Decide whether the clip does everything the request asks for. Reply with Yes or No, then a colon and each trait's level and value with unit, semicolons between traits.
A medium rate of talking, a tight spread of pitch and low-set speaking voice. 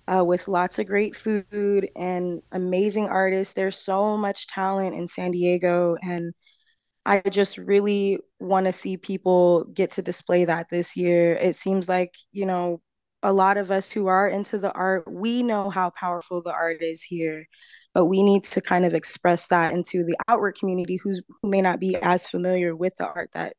No: average, 190 wpm; narrow, 2.0 semitones; medium, 185 Hz